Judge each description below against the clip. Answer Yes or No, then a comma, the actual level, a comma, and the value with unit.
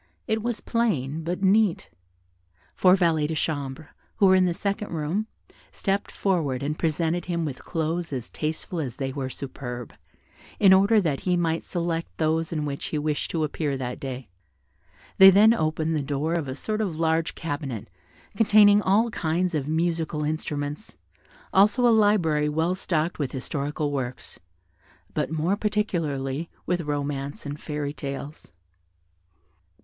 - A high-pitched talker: No, medium, 160 Hz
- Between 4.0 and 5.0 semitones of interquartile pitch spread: Yes, average, 4.3 semitones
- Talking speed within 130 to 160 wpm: Yes, average, 155 wpm